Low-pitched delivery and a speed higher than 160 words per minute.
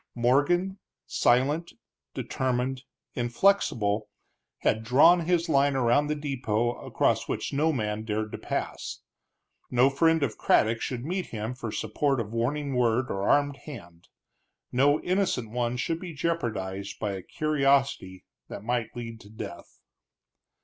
No: low, 125 Hz; slow, 135 wpm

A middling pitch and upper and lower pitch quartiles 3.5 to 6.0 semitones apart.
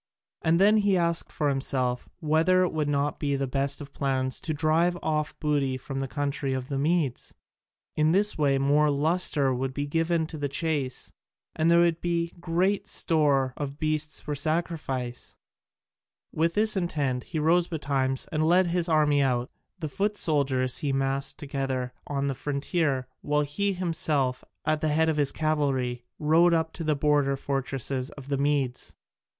No: medium, 150 Hz; average, 3.1 semitones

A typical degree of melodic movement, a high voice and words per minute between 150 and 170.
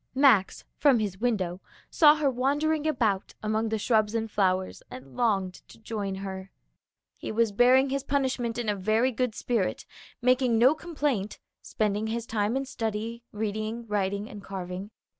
Yes: average, 3.9 semitones; high, 220 Hz; average, 160 wpm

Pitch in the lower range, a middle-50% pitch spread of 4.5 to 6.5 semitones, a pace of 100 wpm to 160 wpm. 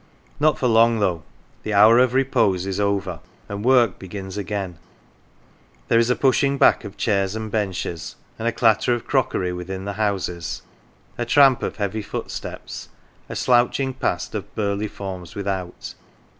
No: low, 105 Hz; average, 3.7 semitones; average, 155 wpm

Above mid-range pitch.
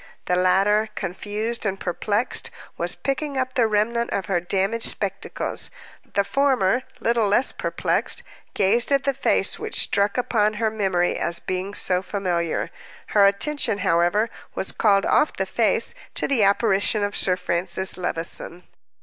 Yes: high, 205 Hz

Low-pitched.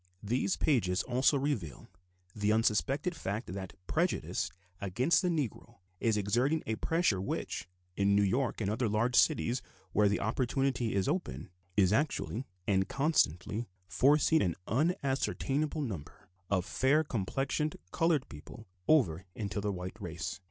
Yes: low, 115 Hz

